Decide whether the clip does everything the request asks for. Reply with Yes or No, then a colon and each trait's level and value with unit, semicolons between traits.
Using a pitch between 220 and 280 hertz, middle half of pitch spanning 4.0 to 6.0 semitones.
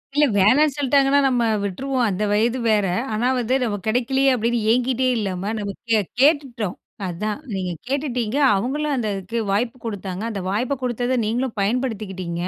Yes: high, 235 Hz; average, 4.3 semitones